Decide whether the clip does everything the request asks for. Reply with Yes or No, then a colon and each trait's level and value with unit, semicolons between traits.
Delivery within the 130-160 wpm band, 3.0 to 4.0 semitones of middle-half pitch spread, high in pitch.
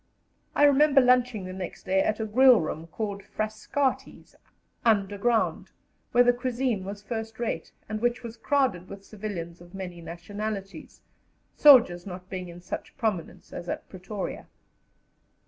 No: average, 145 wpm; average, 4.6 semitones; high, 210 Hz